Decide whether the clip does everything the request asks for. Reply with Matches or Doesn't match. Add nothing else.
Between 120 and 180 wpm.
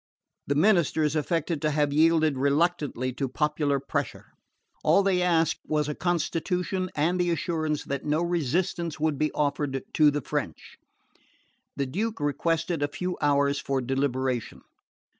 Matches